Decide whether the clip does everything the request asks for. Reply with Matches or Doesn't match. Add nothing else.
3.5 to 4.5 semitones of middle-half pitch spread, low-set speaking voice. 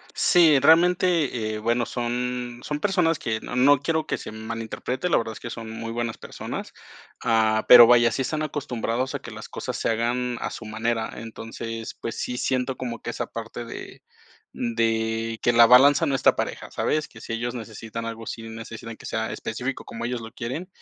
Doesn't match